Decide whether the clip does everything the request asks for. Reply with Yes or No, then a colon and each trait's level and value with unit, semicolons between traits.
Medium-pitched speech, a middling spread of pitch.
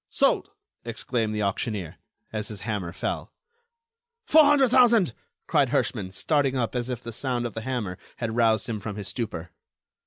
No: low, 115 Hz; average, 3.8 semitones